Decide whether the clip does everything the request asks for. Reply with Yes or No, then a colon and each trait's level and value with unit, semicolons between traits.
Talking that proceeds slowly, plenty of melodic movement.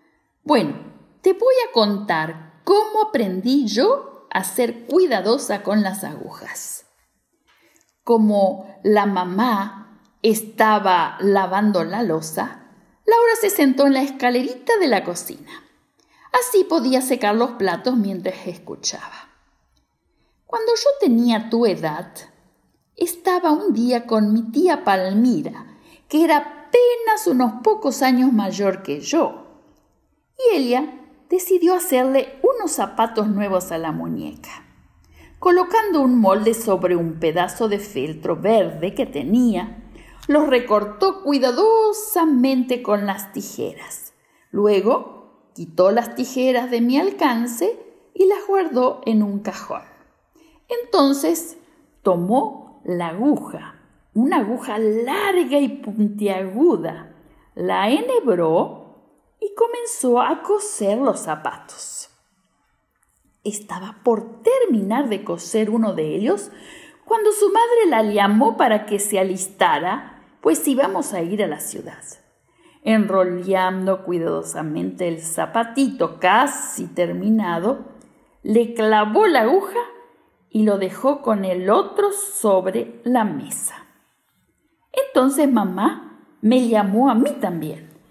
Yes: slow, 110 wpm; wide, 8.0 semitones